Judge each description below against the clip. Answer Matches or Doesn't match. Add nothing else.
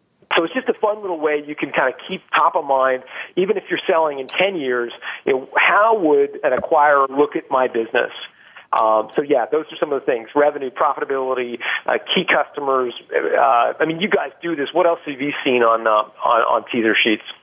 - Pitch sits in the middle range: Matches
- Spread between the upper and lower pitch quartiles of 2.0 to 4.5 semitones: Doesn't match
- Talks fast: Matches